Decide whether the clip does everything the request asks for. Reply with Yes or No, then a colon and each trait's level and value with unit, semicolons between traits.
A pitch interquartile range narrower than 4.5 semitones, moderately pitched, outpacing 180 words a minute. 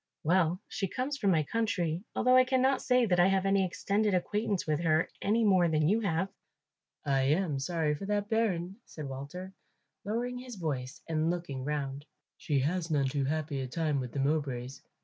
No: wide, 5.6 semitones; medium, 170 Hz; average, 190 wpm